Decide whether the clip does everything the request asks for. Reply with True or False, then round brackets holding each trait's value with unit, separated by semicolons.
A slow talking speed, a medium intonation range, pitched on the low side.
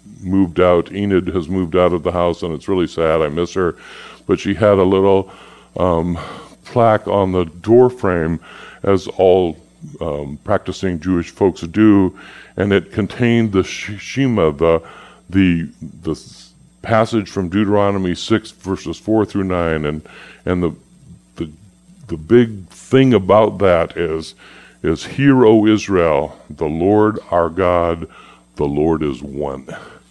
False (145 wpm; 3.4 semitones; 95 Hz)